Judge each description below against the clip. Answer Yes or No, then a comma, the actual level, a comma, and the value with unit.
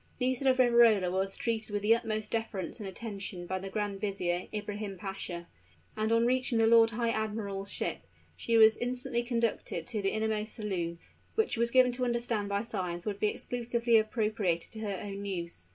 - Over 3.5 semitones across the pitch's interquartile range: No, average, 3.0 semitones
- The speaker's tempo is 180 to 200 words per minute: Yes, average, 185 wpm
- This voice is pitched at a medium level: No, high, 215 Hz